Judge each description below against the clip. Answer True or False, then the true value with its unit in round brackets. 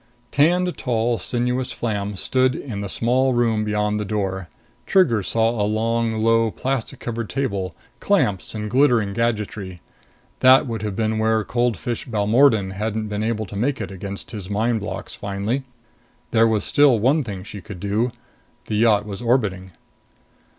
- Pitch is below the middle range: True (110 Hz)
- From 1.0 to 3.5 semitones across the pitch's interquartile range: True (2.8 semitones)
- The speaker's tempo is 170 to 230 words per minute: False (160 wpm)